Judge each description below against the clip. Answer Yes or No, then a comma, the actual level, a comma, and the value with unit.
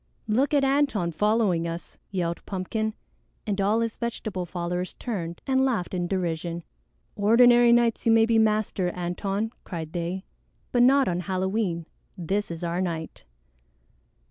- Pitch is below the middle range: No, high, 195 Hz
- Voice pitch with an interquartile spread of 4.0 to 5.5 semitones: Yes, average, 4.6 semitones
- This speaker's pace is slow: No, average, 145 wpm